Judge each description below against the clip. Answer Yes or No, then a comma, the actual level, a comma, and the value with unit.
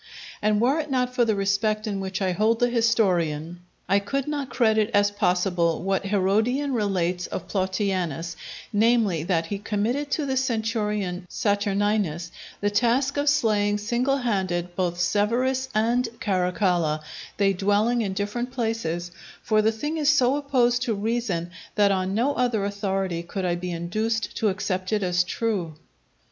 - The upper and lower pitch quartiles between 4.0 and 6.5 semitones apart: Yes, average, 4.3 semitones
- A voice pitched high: Yes, high, 205 Hz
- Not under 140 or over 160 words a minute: Yes, average, 155 wpm